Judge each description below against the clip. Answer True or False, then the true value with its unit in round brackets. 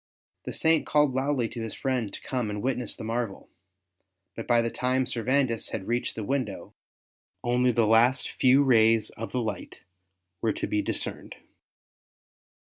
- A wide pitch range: False (2.6 semitones)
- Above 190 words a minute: False (160 wpm)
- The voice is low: True (120 Hz)